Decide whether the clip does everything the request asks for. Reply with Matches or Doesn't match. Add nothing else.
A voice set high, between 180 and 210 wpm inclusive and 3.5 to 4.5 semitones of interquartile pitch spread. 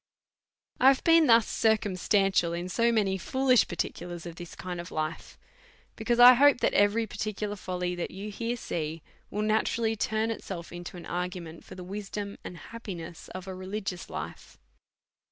Doesn't match